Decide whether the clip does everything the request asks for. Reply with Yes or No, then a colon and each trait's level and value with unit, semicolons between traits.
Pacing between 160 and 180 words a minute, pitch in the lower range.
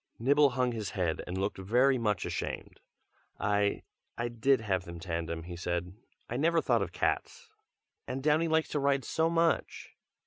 Yes: average, 170 wpm; low, 120 Hz